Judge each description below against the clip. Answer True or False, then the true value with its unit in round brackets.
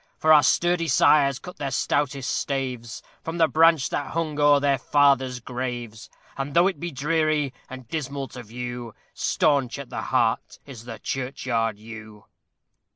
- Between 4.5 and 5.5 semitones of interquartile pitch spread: False (3.5 semitones)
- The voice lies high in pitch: False (135 Hz)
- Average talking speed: True (160 wpm)